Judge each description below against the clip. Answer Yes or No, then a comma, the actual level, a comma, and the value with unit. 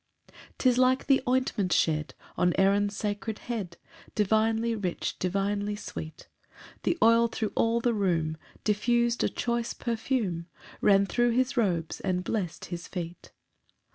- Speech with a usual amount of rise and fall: Yes, average, 4.3 semitones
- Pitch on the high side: Yes, high, 210 Hz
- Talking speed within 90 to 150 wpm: Yes, average, 140 wpm